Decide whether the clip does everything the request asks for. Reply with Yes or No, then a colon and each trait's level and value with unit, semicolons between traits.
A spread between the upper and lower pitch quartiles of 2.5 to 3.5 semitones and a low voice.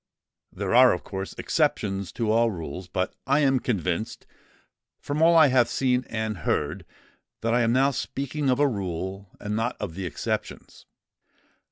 No: wide, 5.4 semitones; low, 115 Hz